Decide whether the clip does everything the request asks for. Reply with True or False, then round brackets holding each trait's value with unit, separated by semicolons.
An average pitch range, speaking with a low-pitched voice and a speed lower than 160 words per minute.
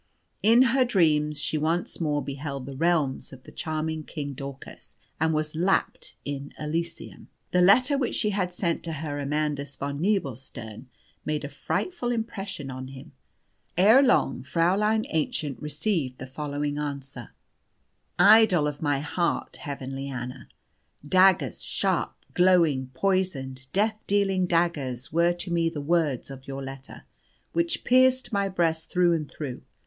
False (4.9 semitones; 155 Hz; 145 wpm)